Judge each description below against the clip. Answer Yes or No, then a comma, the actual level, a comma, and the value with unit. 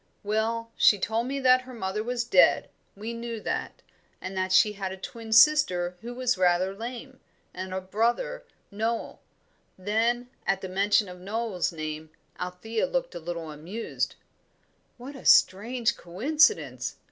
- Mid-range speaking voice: No, high, 220 Hz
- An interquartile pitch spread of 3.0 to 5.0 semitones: Yes, average, 4.4 semitones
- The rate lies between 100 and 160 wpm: Yes, average, 150 wpm